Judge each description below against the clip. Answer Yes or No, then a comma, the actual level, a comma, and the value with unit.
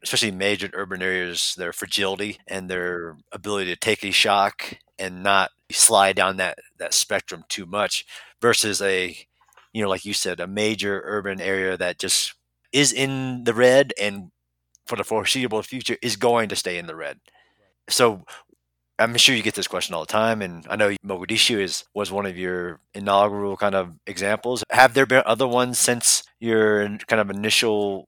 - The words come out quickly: No, average, 180 wpm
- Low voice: Yes, low, 100 Hz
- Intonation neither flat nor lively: Yes, average, 3.0 semitones